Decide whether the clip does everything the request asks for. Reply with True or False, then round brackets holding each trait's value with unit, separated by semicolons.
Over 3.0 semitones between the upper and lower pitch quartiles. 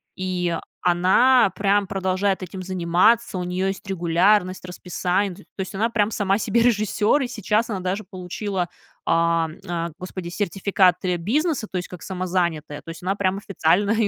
False (2.4 semitones)